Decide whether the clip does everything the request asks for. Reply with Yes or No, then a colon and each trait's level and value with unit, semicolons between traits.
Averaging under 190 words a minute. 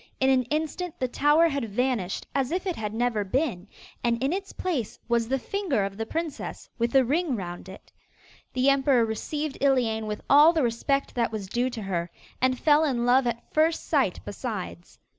No: average, 195 wpm